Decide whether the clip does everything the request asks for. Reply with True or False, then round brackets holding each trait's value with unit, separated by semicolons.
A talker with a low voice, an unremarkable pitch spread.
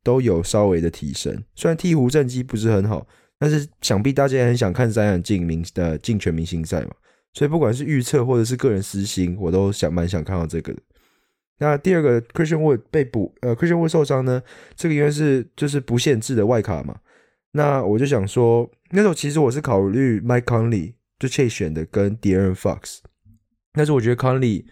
False (120 Hz; 6.3 semitones)